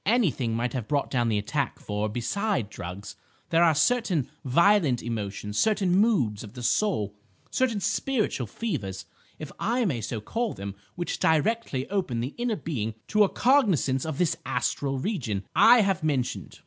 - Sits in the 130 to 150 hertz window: Yes, medium, 140 Hz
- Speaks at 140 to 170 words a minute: Yes, average, 160 wpm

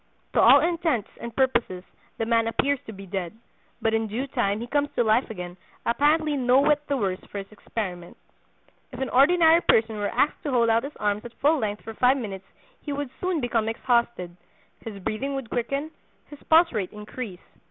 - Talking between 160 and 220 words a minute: Yes, average, 195 wpm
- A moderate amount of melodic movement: Yes, average, 4.9 semitones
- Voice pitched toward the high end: Yes, high, 235 Hz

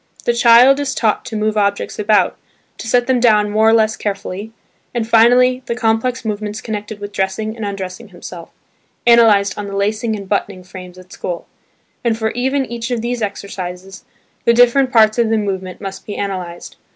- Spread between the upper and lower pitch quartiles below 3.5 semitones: Yes, average, 2.9 semitones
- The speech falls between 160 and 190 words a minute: Yes, average, 185 wpm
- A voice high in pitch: Yes, high, 215 Hz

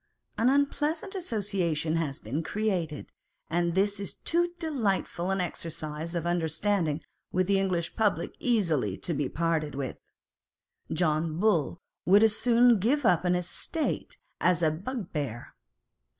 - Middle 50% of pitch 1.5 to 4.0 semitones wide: No, average, 5.3 semitones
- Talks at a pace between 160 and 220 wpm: No, slow, 135 wpm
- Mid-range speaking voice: Yes, medium, 180 Hz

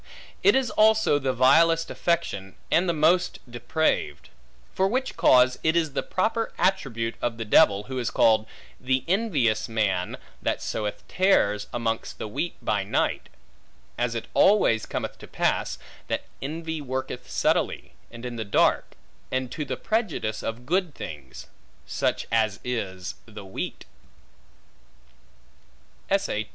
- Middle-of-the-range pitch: No, low, 125 Hz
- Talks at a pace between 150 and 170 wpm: No, average, 140 wpm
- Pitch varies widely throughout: Yes, wide, 7.2 semitones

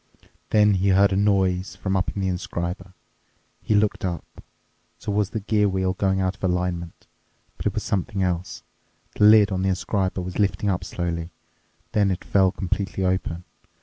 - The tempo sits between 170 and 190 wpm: Yes, average, 180 wpm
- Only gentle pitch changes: Yes, narrow, 1.8 semitones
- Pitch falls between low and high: No, very low, 95 Hz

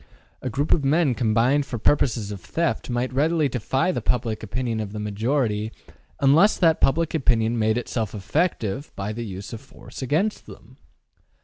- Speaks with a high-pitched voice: No, low, 120 Hz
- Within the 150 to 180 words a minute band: Yes, average, 170 wpm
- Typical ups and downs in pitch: Yes, average, 5.0 semitones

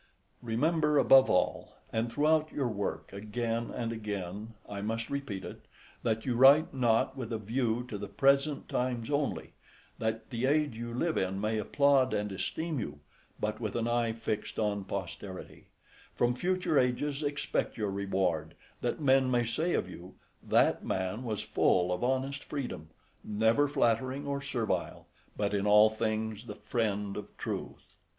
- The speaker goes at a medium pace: Yes, average, 160 wpm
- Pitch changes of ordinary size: Yes, average, 4.5 semitones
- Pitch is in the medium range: No, low, 115 Hz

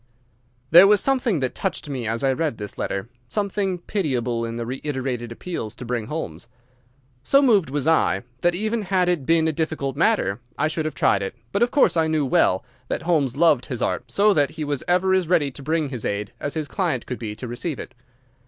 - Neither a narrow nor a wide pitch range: No, wide, 6.2 semitones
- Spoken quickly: Yes, fast, 220 wpm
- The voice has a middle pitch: Yes, medium, 150 Hz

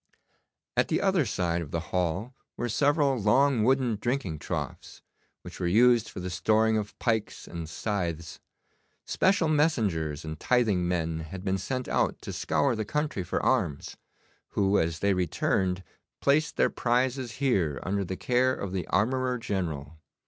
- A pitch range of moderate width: No, wide, 6.5 semitones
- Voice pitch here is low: Yes, low, 105 Hz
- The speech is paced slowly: No, average, 155 wpm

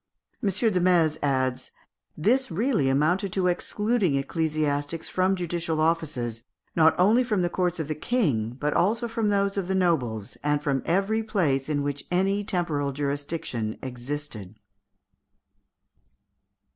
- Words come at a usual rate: No, slow, 130 wpm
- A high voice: No, medium, 165 Hz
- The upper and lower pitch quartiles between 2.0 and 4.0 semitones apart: No, average, 5.2 semitones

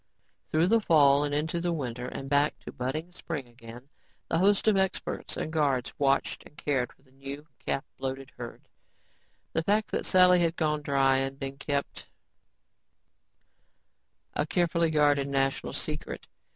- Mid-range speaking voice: Yes, medium, 145 Hz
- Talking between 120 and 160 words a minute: Yes, average, 155 wpm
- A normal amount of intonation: Yes, average, 3.3 semitones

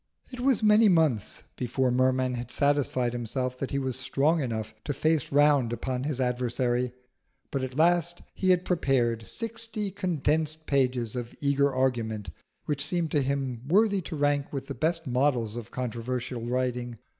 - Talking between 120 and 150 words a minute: No, average, 160 wpm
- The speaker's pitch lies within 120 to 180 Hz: Yes, low, 135 Hz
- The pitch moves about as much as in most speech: Yes, average, 4.1 semitones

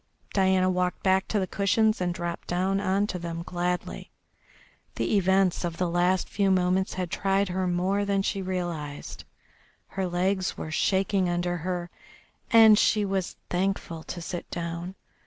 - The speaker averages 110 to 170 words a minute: Yes, average, 155 wpm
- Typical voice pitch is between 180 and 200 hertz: Yes, medium, 185 Hz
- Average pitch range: No, narrow, 1.7 semitones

